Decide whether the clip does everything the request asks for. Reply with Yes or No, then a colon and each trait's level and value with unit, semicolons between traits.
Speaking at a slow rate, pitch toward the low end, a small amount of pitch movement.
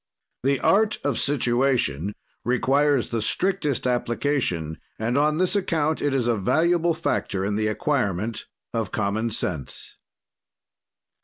No: slow, 125 wpm; low, 125 Hz; wide, 5.5 semitones